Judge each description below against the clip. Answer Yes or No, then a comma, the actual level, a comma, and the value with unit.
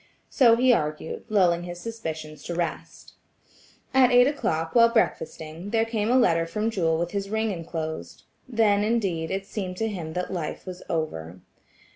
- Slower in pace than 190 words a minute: Yes, average, 165 wpm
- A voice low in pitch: No, medium, 185 Hz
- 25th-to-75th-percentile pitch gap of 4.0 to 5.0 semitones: No, wide, 5.5 semitones